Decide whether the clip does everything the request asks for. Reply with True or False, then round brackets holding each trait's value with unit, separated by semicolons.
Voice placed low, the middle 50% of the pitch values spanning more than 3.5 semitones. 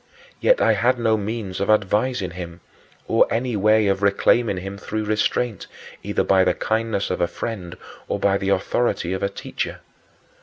False (100 Hz; 2.8 semitones)